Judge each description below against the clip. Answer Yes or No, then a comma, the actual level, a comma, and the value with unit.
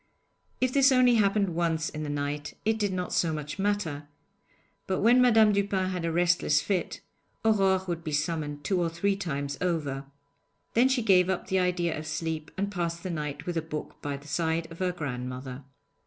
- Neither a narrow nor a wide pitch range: Yes, average, 4.4 semitones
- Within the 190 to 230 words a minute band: Yes, average, 195 wpm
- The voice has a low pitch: No, medium, 170 Hz